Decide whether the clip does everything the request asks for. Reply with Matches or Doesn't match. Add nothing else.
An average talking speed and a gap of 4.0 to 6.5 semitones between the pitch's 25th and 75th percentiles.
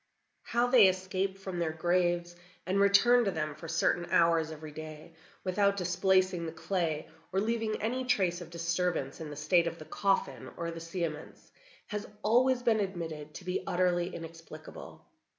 Doesn't match